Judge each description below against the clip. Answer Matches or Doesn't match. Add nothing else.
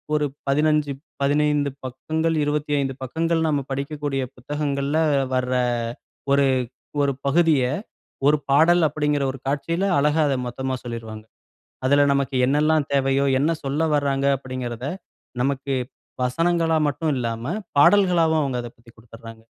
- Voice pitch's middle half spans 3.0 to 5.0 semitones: Doesn't match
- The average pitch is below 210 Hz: Matches